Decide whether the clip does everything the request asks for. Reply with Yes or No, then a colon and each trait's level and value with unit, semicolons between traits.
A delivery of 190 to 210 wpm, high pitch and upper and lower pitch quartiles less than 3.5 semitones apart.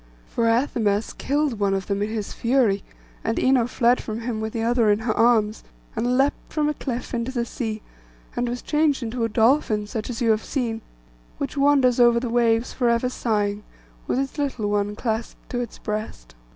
Yes: average, 200 wpm; high, 235 Hz; narrow, 2.6 semitones